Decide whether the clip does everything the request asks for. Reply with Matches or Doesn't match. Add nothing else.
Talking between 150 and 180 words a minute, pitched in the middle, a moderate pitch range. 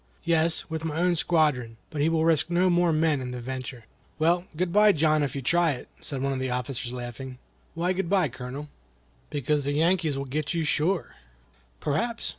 Doesn't match